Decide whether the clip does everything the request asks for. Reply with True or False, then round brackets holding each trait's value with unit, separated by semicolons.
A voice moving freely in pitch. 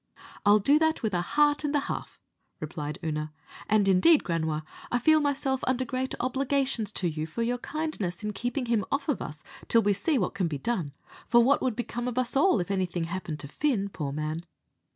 True (7.5 semitones)